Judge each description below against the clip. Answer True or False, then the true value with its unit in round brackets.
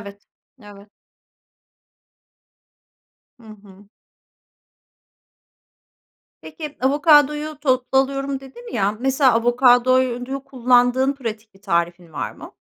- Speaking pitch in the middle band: False (250 Hz)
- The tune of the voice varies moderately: True (4.3 semitones)